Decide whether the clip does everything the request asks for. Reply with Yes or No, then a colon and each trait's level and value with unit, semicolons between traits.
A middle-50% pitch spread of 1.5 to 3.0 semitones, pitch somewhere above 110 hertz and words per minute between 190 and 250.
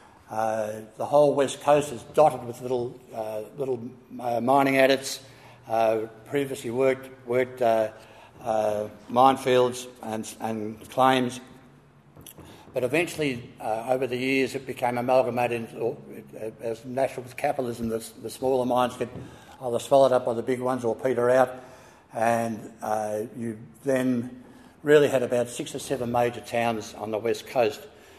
No: narrow, 2.6 semitones; low, 125 Hz; average, 150 wpm